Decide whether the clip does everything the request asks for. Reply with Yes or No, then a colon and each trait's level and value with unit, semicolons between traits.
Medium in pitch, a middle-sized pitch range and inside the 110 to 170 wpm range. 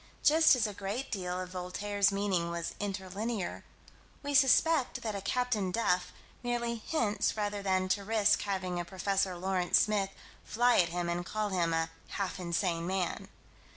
No: high, 195 Hz; average, 3.1 semitones; average, 165 wpm